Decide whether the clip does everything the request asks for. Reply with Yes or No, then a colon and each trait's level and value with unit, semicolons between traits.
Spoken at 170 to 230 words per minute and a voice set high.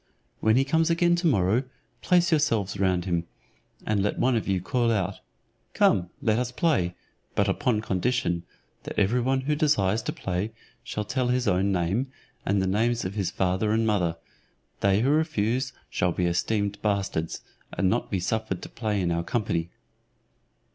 No: average, 175 wpm; low, 105 Hz